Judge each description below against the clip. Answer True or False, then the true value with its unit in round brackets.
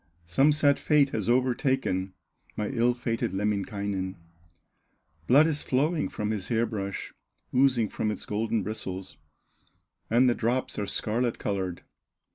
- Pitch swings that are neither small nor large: True (4.3 semitones)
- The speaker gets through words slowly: True (130 wpm)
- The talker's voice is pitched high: False (115 Hz)